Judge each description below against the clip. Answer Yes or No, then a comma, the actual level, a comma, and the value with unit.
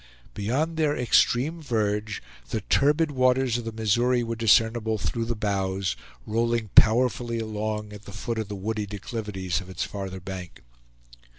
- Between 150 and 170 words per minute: Yes, average, 155 wpm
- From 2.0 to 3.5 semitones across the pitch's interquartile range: Yes, average, 2.8 semitones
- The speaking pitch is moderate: No, low, 110 Hz